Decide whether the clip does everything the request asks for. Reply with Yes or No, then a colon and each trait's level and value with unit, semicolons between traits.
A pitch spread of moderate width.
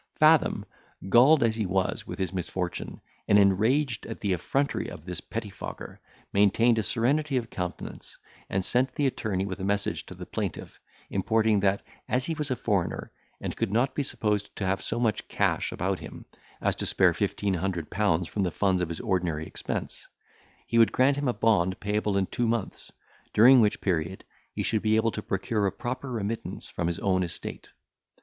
Yes: average, 3.8 semitones